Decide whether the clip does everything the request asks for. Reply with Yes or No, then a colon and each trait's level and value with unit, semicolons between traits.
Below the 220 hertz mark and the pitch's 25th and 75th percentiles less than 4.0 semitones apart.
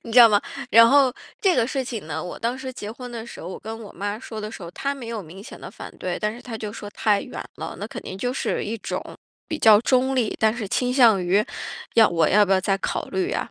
No: high, 225 Hz; average, 3.4 semitones